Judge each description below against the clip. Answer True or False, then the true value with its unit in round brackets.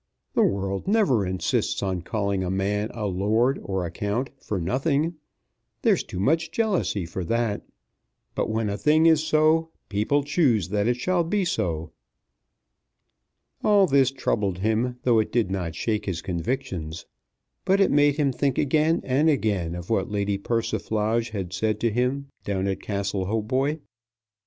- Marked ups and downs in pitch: True (6.2 semitones)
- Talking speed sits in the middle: True (160 wpm)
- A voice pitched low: True (110 Hz)